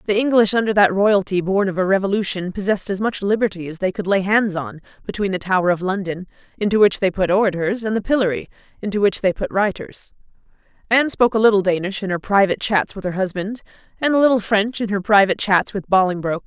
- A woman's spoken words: Yes, female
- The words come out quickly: Yes, fast, 215 wpm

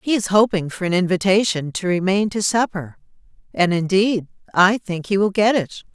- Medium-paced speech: Yes, average, 180 wpm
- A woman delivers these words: Yes, female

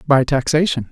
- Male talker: Yes, male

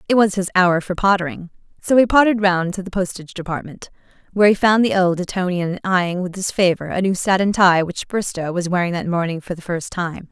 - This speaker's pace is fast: Yes, fast, 215 wpm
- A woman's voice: Yes, female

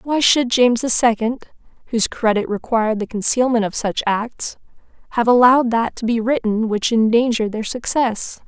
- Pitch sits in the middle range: No, high, 230 Hz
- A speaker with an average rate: Yes, average, 165 wpm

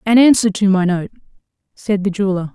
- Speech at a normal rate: Yes, average, 190 wpm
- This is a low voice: No, high, 200 Hz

